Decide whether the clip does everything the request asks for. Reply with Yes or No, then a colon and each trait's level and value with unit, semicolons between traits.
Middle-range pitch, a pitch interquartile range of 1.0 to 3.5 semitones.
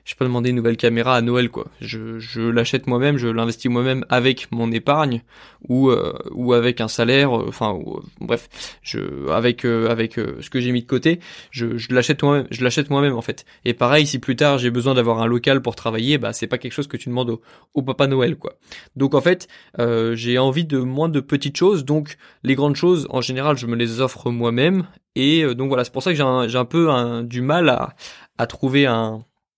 No: low, 125 Hz; average, 3.1 semitones